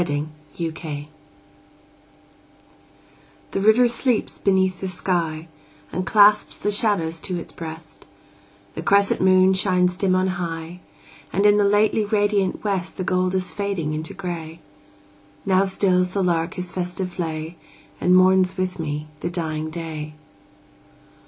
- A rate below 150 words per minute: Yes, average, 140 wpm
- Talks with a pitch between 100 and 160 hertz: No, medium, 185 Hz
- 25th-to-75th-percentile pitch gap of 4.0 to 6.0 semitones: No, average, 3.0 semitones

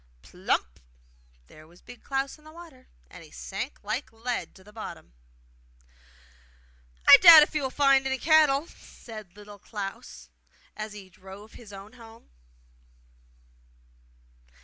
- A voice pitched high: Yes, high, 225 Hz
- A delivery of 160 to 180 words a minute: No, slow, 135 wpm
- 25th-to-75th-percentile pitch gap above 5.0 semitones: Yes, wide, 5.6 semitones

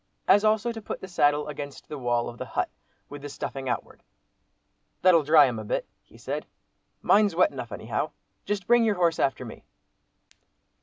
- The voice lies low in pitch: No, medium, 150 Hz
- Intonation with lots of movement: Yes, wide, 6.9 semitones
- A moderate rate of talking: Yes, average, 185 wpm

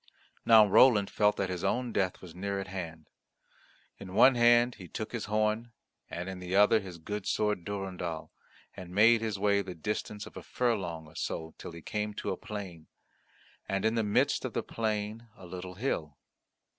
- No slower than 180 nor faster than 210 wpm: Yes, average, 190 wpm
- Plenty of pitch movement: No, average, 3.1 semitones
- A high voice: No, low, 100 Hz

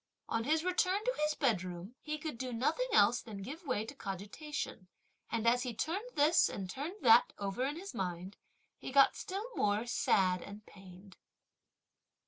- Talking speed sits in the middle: Yes, average, 170 wpm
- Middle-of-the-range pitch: No, high, 240 Hz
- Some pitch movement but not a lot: No, wide, 7.4 semitones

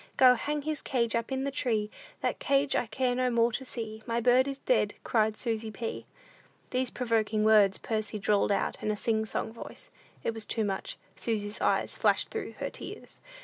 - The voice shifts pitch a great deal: No, average, 2.8 semitones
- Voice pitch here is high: Yes, high, 230 Hz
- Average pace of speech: Yes, average, 195 wpm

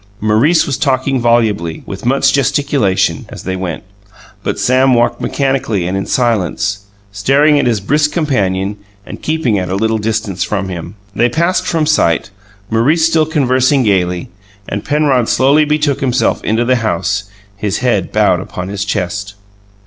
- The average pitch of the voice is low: Yes, low, 115 Hz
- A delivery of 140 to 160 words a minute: Yes, average, 155 wpm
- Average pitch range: No, wide, 5.8 semitones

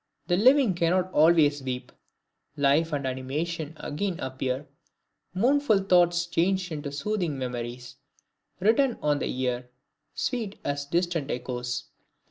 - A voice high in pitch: No, medium, 160 Hz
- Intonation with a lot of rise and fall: Yes, wide, 5.9 semitones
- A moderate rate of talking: No, slow, 115 wpm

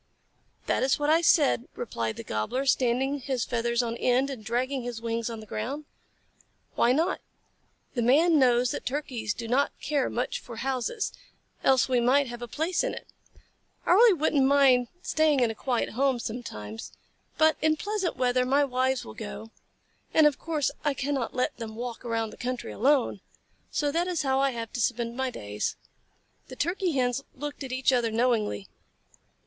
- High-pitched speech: Yes, very high, 255 Hz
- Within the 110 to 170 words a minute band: No, average, 180 wpm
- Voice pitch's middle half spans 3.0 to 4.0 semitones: Yes, average, 3.4 semitones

